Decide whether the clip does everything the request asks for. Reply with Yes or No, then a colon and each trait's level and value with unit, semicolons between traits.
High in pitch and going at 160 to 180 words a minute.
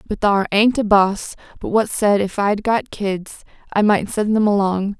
No: high, 205 Hz; fast, 205 wpm